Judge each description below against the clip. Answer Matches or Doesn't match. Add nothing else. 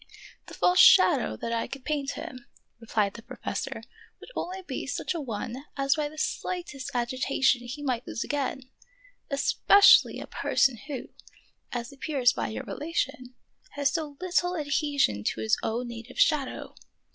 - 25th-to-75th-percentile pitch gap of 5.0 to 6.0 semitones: Doesn't match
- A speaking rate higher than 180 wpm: Doesn't match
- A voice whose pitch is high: Matches